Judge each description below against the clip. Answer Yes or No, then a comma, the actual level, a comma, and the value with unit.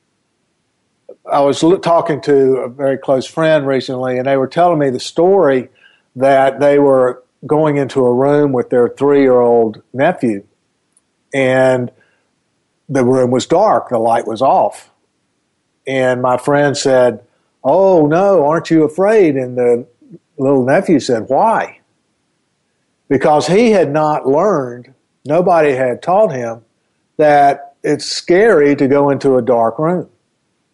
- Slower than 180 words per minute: Yes, average, 140 wpm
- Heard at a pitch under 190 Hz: Yes, low, 135 Hz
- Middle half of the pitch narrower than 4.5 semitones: Yes, average, 3.2 semitones